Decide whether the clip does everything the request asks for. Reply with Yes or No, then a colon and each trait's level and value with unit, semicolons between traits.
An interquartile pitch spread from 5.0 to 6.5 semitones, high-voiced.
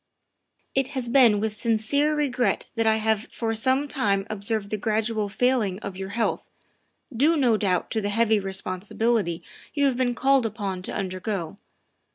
No: average, 3.8 semitones; high, 220 Hz